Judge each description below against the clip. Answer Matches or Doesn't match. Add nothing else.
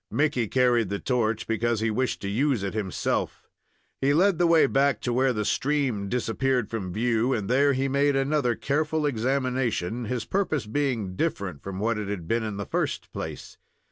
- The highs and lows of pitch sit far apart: Doesn't match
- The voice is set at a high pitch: Doesn't match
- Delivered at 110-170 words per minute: Doesn't match